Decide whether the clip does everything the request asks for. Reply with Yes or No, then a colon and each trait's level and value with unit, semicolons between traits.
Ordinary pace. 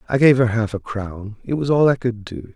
No: fast, 280 wpm